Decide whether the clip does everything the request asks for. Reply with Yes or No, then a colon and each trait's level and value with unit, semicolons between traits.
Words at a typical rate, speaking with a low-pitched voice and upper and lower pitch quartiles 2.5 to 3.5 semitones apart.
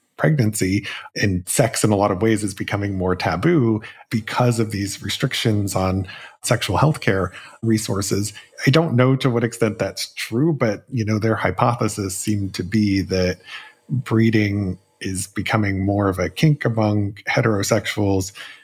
Yes: average, 150 wpm; low, 105 Hz; average, 3.2 semitones